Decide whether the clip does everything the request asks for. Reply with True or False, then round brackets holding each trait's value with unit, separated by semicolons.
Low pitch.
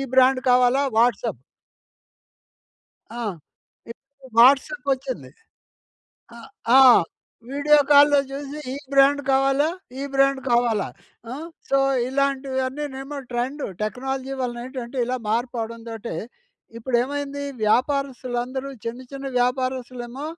False (265 Hz)